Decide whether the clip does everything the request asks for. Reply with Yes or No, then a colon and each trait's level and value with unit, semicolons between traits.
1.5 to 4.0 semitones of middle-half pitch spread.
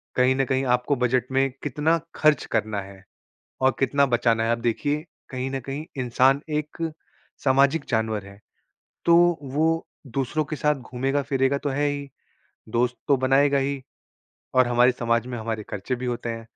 Yes: average, 2.9 semitones